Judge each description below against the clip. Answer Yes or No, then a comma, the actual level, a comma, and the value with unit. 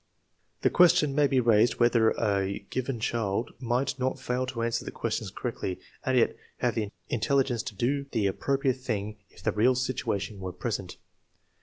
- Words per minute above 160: Yes, average, 170 wpm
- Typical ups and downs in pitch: Yes, average, 3.4 semitones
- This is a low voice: Yes, low, 120 Hz